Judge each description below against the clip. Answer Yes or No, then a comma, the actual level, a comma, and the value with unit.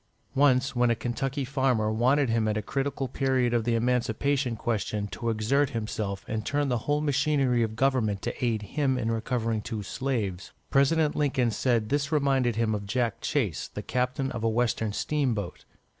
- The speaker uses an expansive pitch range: No, average, 3.6 semitones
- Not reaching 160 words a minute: No, average, 175 wpm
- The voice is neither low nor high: No, low, 120 Hz